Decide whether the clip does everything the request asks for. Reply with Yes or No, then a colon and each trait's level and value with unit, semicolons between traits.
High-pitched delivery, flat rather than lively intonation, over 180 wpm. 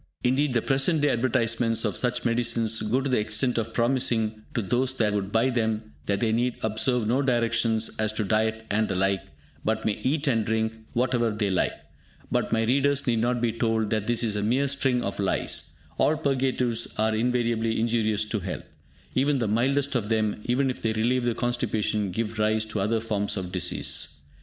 No: low, 115 Hz; narrow, 2.3 semitones; average, 195 wpm